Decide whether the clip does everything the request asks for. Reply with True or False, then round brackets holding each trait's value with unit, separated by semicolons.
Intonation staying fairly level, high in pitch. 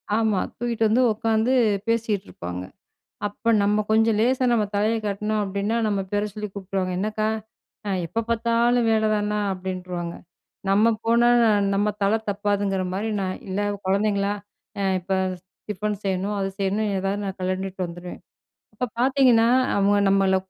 True (2.3 semitones; 205 Hz)